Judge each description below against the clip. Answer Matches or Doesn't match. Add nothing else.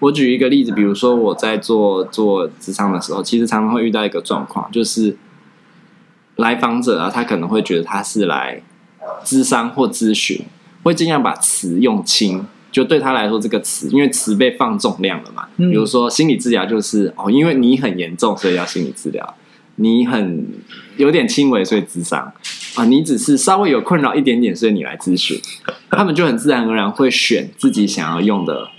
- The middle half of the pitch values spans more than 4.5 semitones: Matches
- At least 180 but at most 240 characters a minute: Doesn't match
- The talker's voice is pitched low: Matches